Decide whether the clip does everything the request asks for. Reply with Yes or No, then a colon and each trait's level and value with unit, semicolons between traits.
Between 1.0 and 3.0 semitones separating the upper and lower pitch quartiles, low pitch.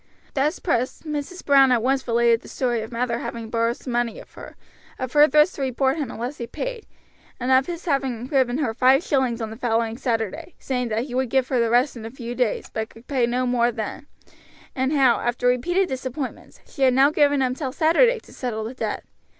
No: average, 2.7 semitones; very high, 255 Hz